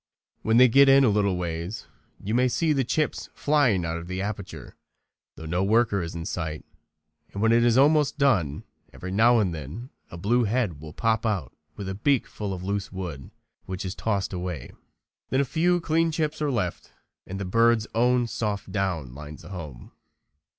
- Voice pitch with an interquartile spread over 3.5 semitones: Yes, wide, 5.5 semitones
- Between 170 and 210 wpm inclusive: Yes, average, 190 wpm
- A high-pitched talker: No, low, 105 Hz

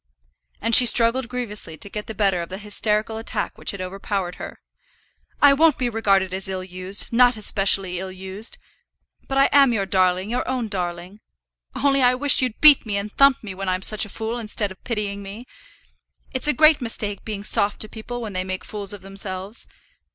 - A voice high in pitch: Yes, high, 210 Hz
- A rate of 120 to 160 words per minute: No, fast, 205 wpm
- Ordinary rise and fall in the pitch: Yes, average, 4.0 semitones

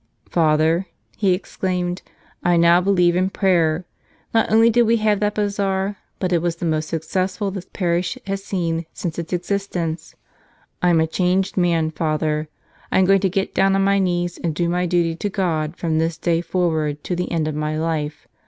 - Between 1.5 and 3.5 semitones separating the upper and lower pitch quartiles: Yes, average, 2.9 semitones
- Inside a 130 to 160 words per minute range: No, average, 190 wpm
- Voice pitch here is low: No, medium, 175 Hz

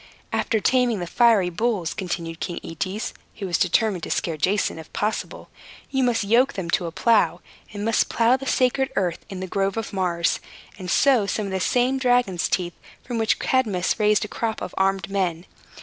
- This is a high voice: Yes, high, 200 Hz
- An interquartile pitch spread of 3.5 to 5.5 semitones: Yes, average, 4.4 semitones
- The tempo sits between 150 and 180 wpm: No, average, 195 wpm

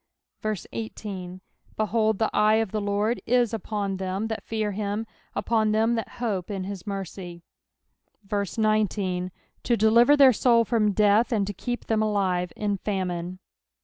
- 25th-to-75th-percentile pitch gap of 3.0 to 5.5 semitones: No, narrow, 2.5 semitones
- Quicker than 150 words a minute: No, average, 145 wpm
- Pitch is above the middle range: Yes, high, 210 Hz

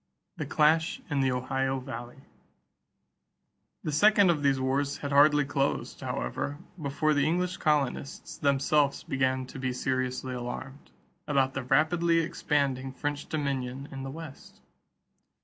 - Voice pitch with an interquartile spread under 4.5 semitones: Yes, narrow, 2.4 semitones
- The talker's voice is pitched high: No, medium, 140 Hz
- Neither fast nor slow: No, slow, 130 wpm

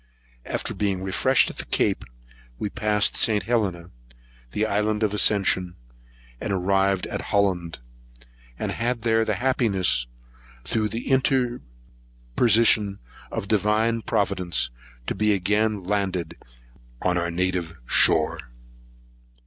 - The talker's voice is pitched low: Yes, low, 100 Hz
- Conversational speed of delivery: No, slow, 110 wpm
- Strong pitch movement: No, average, 3.4 semitones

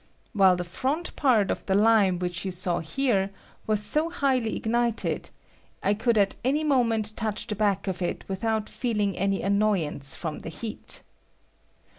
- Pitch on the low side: No, high, 210 Hz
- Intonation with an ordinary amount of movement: Yes, average, 3.6 semitones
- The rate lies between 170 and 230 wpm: No, average, 160 wpm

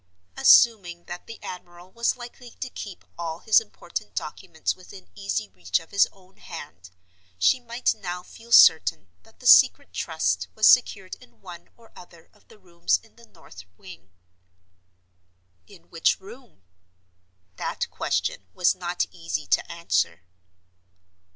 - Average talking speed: Yes, average, 145 wpm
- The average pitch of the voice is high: No, medium, 175 Hz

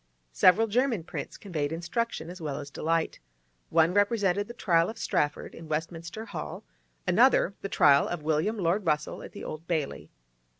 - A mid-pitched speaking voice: Yes, medium, 170 Hz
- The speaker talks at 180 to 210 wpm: No, average, 165 wpm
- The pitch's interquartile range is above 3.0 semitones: Yes, average, 4.5 semitones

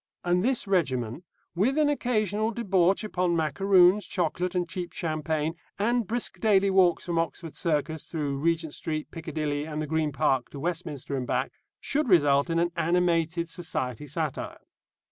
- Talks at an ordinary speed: Yes, average, 155 wpm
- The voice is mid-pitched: Yes, medium, 170 Hz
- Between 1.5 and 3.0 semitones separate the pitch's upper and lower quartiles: No, average, 3.8 semitones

